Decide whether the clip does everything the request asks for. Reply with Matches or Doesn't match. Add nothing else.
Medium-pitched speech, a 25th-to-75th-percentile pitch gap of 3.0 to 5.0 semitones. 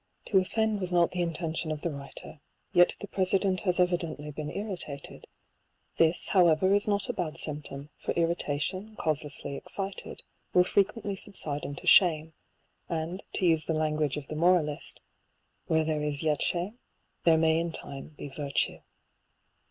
Matches